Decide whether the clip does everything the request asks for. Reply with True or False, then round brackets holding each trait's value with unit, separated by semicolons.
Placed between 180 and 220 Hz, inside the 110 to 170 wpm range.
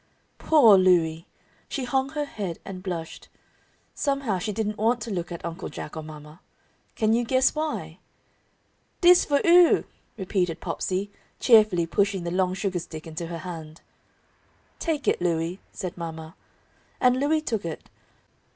True (190 Hz; 150 wpm)